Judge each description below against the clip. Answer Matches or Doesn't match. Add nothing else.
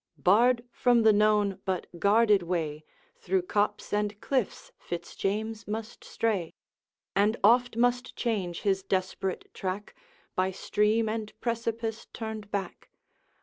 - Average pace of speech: Doesn't match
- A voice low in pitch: Doesn't match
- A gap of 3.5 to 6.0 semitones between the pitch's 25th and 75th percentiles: Doesn't match